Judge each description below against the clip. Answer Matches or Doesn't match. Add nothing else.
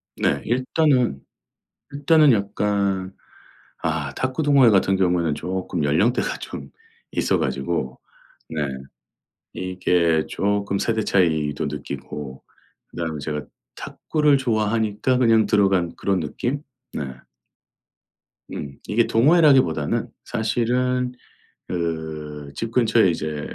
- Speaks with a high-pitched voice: Doesn't match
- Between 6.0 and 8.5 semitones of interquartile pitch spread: Matches